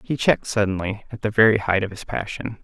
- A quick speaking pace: Yes, fast, 225 wpm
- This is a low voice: Yes, low, 105 Hz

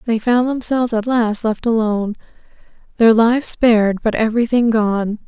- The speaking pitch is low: No, high, 225 Hz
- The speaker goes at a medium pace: Yes, average, 150 wpm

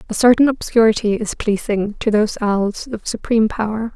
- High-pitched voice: Yes, high, 220 Hz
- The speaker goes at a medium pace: Yes, average, 165 wpm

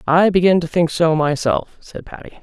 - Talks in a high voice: No, medium, 165 Hz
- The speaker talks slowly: No, average, 200 wpm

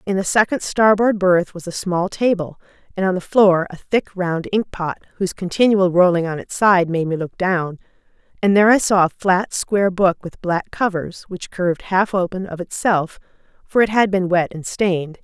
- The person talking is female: Yes, female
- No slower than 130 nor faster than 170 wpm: No, fast, 205 wpm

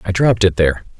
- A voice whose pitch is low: Yes, very low, 95 Hz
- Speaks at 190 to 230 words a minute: No, fast, 240 wpm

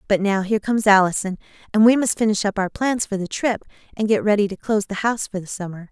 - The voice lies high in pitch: Yes, high, 205 Hz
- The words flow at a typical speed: No, fast, 255 wpm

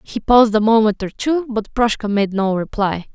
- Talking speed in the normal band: No, fast, 210 wpm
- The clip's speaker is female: Yes, female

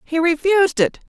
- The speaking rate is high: No, average, 155 wpm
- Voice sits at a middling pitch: No, very high, 335 Hz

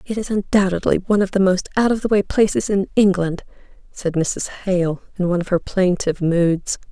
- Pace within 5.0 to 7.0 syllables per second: Yes, 5.5 syllables/s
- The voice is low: No, high, 190 Hz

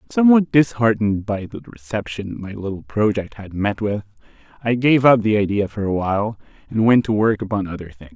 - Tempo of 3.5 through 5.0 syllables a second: No, 5.6 syllables/s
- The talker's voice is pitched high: No, low, 110 Hz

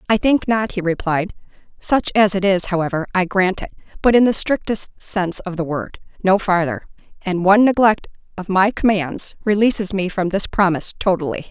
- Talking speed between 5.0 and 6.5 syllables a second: Yes, 5.4 syllables/s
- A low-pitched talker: No, high, 195 Hz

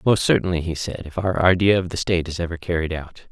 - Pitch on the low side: Yes, very low, 85 Hz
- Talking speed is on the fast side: Yes, fast, 255 wpm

